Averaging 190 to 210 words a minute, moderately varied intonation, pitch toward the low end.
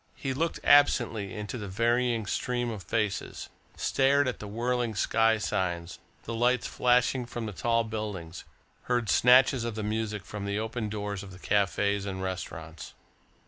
No: average, 160 wpm; average, 3.3 semitones; low, 110 Hz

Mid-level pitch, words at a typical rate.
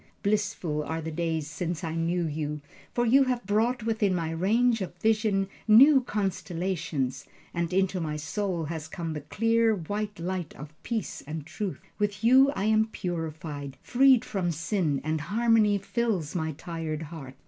Yes: medium, 180 Hz; average, 160 wpm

